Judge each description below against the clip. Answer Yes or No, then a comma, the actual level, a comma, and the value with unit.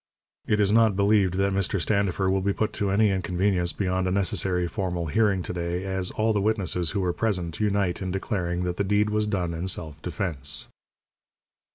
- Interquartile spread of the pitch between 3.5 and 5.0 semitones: No, narrow, 2.4 semitones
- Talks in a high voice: No, very low, 95 Hz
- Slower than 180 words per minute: No, average, 195 wpm